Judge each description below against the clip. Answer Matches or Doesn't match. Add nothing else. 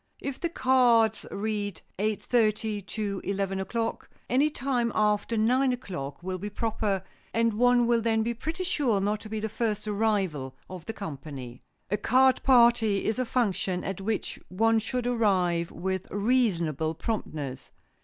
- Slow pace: Doesn't match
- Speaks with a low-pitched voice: Doesn't match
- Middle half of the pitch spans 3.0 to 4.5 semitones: Matches